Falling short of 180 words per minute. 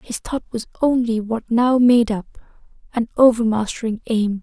Yes: average, 150 wpm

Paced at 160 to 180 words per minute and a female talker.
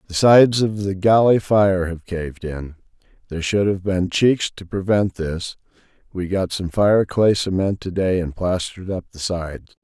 No: average, 175 wpm; male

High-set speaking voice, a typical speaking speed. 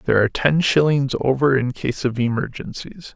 No: low, 135 Hz; average, 170 wpm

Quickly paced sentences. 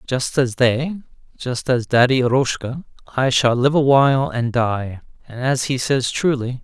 No: average, 165 wpm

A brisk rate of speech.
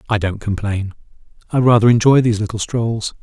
No: average, 165 wpm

